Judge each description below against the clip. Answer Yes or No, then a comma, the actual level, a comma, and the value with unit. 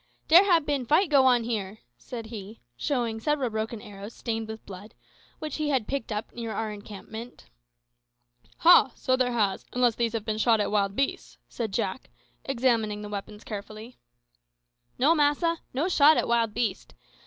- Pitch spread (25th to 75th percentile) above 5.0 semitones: No, average, 4.0 semitones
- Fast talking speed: No, average, 170 wpm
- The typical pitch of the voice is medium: No, high, 230 Hz